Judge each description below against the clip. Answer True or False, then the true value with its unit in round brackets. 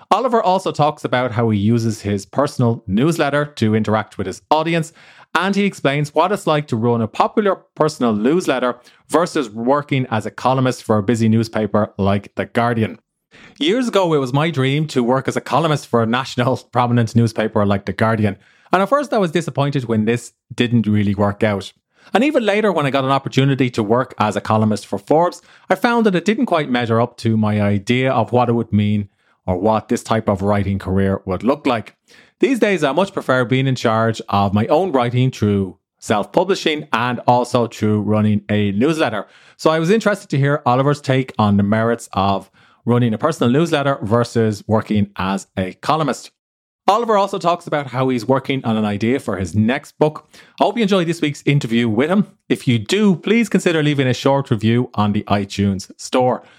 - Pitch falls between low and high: False (125 Hz)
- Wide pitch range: True (5.8 semitones)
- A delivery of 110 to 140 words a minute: False (200 wpm)